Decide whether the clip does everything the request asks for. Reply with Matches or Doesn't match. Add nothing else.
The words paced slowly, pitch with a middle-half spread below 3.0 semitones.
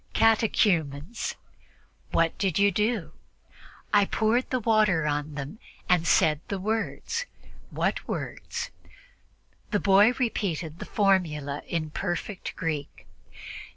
Doesn't match